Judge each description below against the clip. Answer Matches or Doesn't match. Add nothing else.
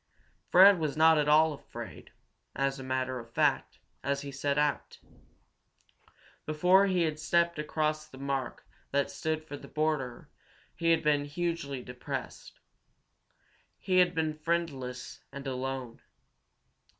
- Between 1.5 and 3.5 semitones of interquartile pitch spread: Matches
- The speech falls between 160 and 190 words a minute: Doesn't match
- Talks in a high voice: Doesn't match